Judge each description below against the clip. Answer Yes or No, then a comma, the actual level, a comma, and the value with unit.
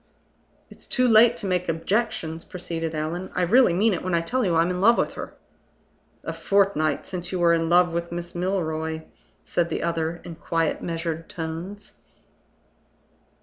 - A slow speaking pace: No, average, 170 wpm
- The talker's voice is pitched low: No, medium, 175 Hz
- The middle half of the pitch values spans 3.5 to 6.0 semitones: No, narrow, 2.6 semitones